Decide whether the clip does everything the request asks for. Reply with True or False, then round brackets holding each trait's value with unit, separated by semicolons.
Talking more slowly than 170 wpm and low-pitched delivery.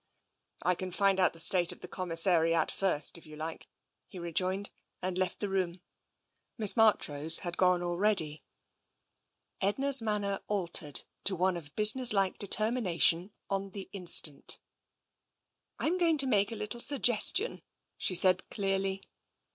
False (145 wpm; 190 Hz)